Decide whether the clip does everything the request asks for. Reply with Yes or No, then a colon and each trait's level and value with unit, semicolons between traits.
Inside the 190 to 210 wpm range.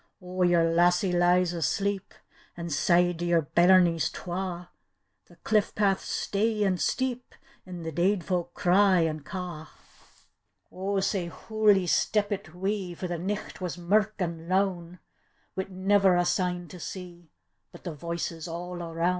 No: average, 145 wpm